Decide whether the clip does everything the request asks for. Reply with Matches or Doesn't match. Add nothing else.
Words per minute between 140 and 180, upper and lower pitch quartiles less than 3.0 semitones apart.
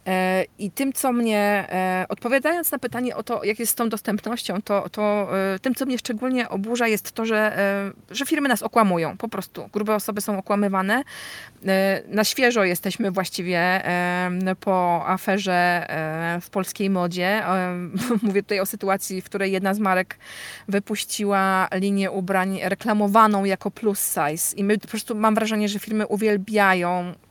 Matches